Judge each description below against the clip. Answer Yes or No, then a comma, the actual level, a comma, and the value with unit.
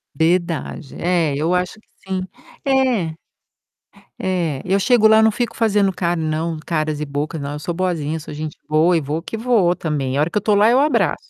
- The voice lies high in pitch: No, medium, 175 Hz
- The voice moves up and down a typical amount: Yes, average, 4.9 semitones